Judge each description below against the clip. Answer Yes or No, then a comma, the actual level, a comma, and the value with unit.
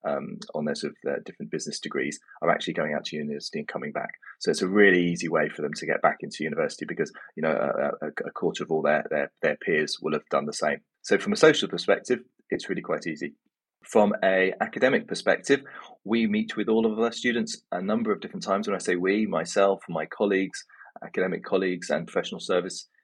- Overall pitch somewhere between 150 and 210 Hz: No, low, 100 Hz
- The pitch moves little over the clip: No, average, 3.7 semitones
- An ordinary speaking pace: No, fast, 225 wpm